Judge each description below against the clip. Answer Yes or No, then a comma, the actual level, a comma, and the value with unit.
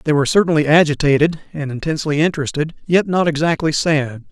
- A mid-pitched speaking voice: Yes, medium, 155 Hz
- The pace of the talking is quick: No, average, 155 wpm